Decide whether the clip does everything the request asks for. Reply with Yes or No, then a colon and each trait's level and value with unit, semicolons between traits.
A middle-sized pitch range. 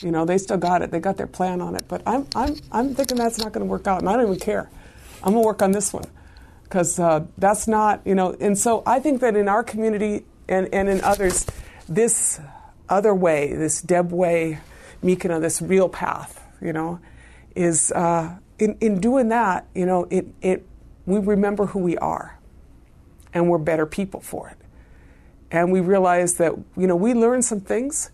Yes: average, 3.9 semitones